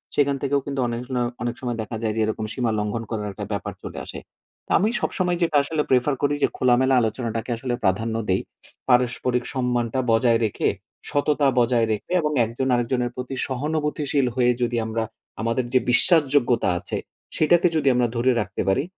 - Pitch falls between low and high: No, low, 125 Hz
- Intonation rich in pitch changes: No, average, 3.4 semitones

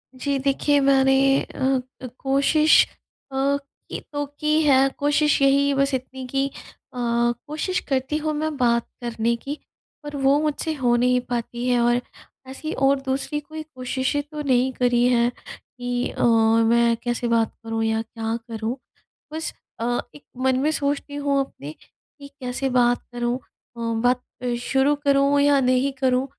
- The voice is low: No, very high, 265 Hz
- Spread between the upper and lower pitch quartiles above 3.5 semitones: No, average, 2.8 semitones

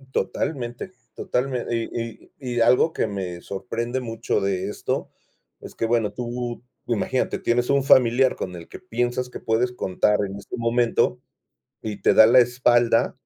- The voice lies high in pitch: No, low, 120 Hz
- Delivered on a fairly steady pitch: Yes, narrow, 1.9 semitones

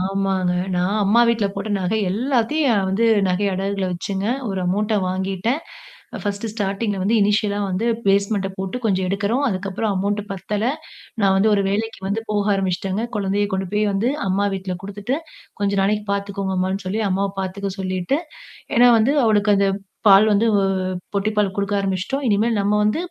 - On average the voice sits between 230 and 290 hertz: No, high, 200 Hz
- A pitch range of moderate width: No, narrow, 1.8 semitones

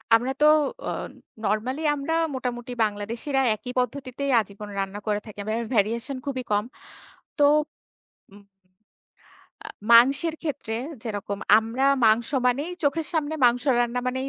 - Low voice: No, high, 245 Hz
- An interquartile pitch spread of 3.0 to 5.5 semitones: Yes, average, 4.2 semitones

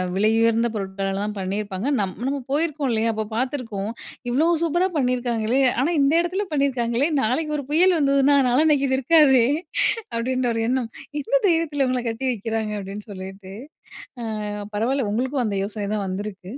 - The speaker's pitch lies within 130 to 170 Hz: No, high, 245 Hz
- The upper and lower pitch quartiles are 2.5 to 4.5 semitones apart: No, average, 4.9 semitones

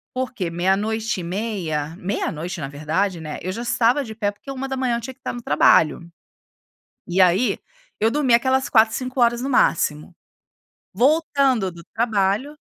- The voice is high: Yes, high, 220 Hz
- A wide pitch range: Yes, wide, 5.9 semitones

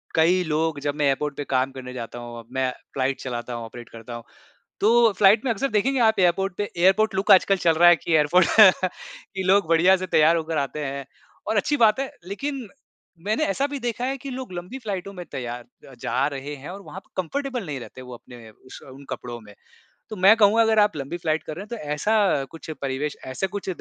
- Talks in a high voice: No, medium, 175 Hz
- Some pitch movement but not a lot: No, wide, 7.3 semitones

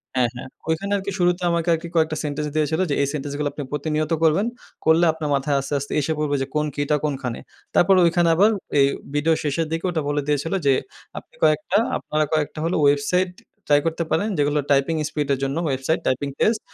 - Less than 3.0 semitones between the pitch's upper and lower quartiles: Yes, narrow, 2.4 semitones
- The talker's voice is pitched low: No, medium, 150 Hz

